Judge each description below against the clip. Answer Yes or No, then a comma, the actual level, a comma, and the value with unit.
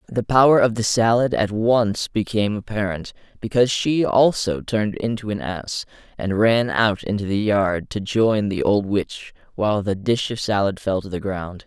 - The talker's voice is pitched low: Yes, low, 105 Hz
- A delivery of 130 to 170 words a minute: No, average, 185 wpm